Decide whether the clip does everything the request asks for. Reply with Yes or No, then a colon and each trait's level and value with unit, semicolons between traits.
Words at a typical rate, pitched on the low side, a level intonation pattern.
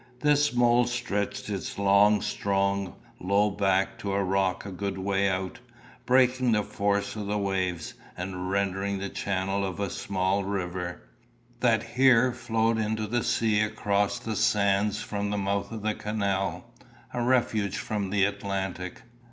Yes: average, 150 wpm; low, 100 Hz; narrow, 1.8 semitones